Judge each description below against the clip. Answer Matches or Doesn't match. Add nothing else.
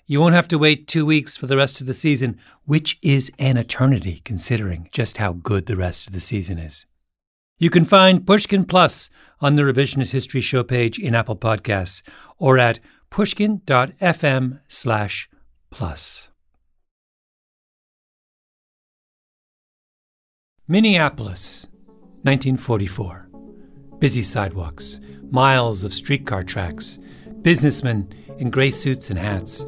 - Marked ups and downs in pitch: Matches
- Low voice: Matches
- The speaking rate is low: Matches